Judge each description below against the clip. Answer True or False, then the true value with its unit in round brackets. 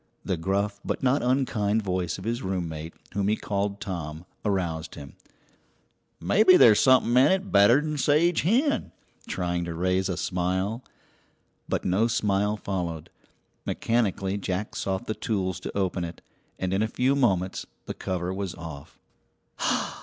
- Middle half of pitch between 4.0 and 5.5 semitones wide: True (4.3 semitones)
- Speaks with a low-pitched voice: True (100 Hz)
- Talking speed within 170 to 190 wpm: False (145 wpm)